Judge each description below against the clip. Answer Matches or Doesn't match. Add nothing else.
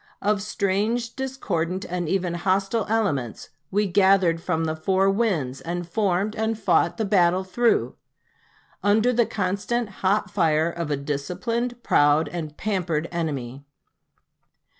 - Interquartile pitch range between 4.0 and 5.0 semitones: Matches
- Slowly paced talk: Matches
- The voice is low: Doesn't match